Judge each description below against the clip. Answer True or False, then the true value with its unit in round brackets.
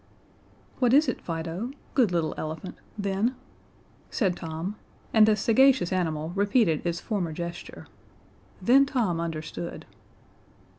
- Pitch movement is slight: False (5.6 semitones)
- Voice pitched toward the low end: False (185 Hz)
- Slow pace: True (115 wpm)